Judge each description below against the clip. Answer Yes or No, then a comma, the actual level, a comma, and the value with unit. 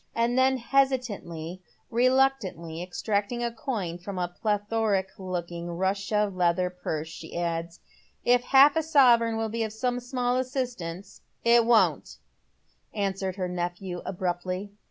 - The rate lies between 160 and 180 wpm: No, average, 140 wpm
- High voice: Yes, high, 205 Hz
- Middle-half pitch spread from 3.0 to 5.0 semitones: No, wide, 5.4 semitones